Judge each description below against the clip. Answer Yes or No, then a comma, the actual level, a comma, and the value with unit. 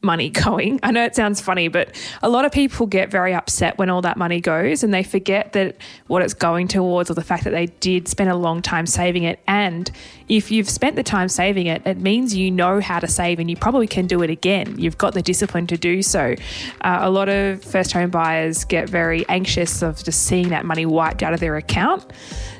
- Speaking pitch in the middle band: Yes, medium, 180 Hz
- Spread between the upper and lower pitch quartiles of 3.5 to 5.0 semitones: No, average, 2.7 semitones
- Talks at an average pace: No, fast, 235 wpm